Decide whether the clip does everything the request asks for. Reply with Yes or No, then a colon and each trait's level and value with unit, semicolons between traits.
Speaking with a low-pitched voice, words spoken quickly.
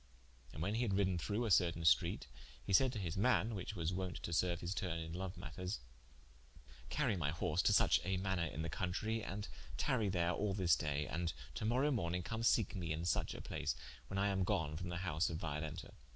Yes: very low, 90 Hz; fast, 225 wpm